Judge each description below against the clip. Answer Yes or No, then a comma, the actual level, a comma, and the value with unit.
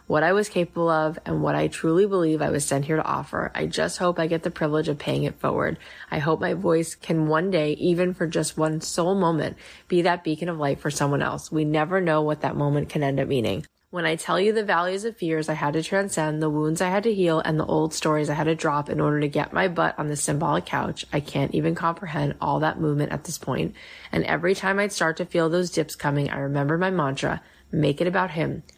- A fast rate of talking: Yes, fast, 255 wpm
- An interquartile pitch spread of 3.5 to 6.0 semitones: No, average, 2.9 semitones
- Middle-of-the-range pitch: Yes, medium, 160 Hz